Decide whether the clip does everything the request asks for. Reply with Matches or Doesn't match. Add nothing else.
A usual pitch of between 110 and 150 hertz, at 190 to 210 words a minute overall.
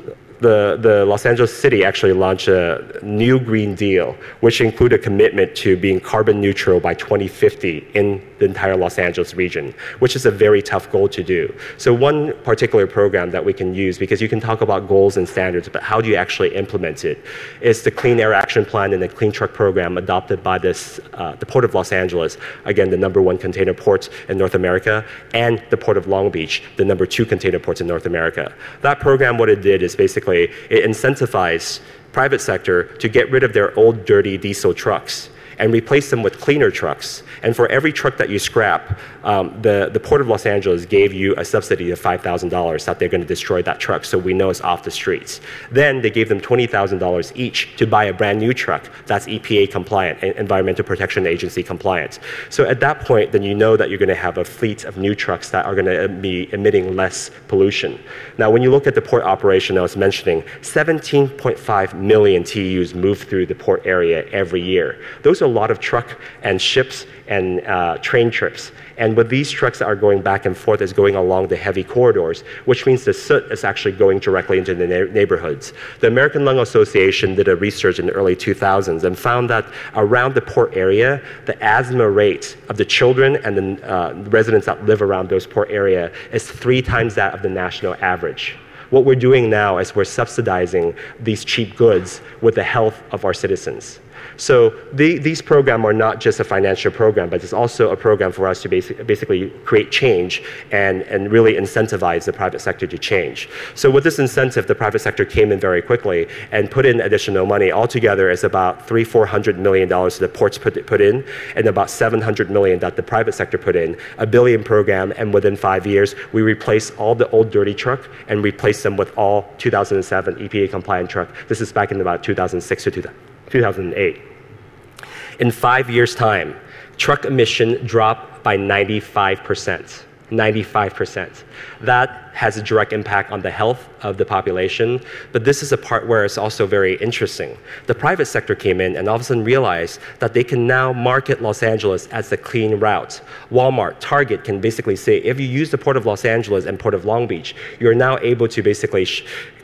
Matches